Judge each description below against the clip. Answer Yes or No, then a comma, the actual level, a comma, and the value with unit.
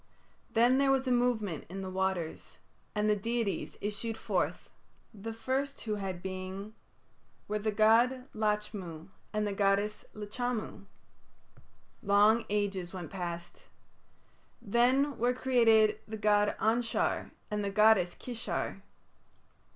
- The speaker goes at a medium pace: No, slow, 120 wpm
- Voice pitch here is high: Yes, high, 210 Hz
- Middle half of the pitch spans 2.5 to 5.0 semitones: Yes, average, 2.9 semitones